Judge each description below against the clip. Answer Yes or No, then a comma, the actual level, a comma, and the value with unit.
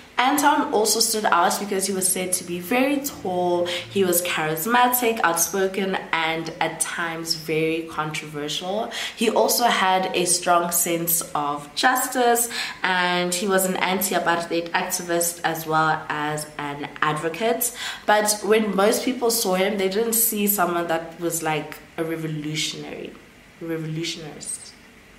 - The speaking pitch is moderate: Yes, medium, 175 Hz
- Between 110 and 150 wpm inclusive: Yes, average, 140 wpm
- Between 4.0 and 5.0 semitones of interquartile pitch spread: Yes, average, 4.4 semitones